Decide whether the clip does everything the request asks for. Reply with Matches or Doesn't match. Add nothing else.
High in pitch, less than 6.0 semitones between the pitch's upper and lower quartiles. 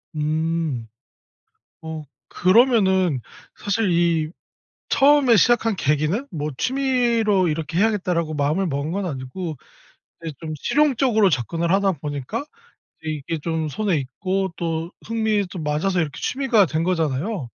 Doesn't match